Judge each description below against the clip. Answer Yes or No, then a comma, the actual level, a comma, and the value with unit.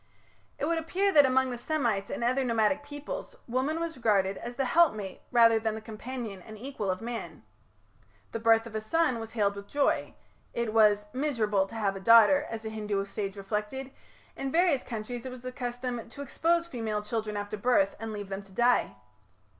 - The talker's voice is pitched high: Yes, high, 230 Hz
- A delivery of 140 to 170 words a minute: No, average, 195 wpm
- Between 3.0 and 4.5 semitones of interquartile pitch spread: Yes, average, 3.9 semitones